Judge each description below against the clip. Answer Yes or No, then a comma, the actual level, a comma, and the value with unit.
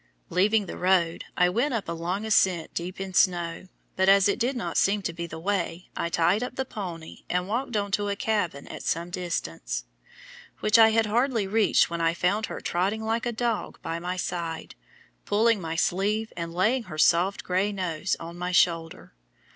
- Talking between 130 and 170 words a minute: No, average, 195 wpm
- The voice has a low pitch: No, medium, 185 Hz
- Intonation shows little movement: No, average, 3.9 semitones